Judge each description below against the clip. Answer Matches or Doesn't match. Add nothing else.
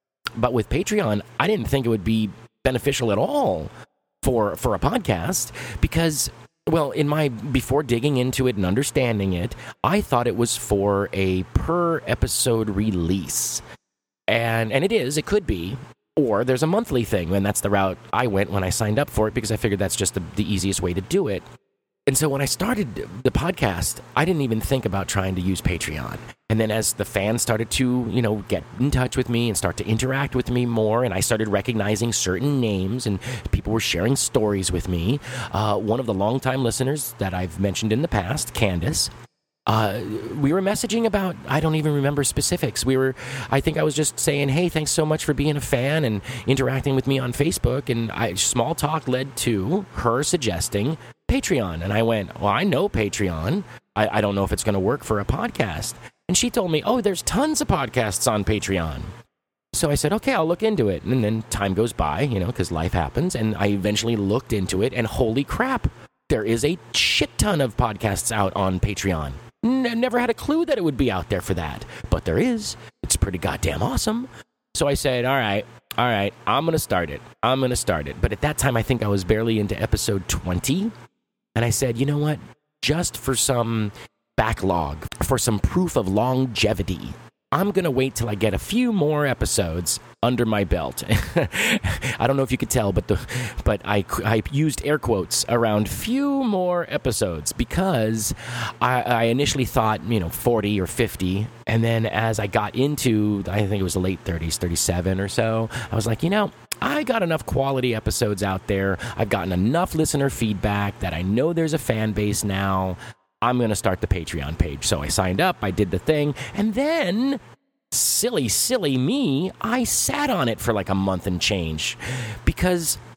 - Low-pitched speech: Matches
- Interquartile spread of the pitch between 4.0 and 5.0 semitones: Doesn't match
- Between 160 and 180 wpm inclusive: Doesn't match